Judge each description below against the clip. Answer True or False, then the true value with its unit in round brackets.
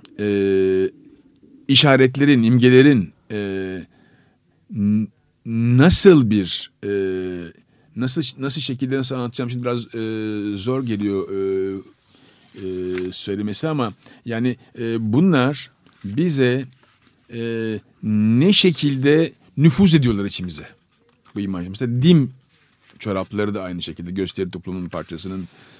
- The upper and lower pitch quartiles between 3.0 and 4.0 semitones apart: False (5.5 semitones)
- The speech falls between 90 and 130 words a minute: True (95 wpm)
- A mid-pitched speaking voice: False (115 Hz)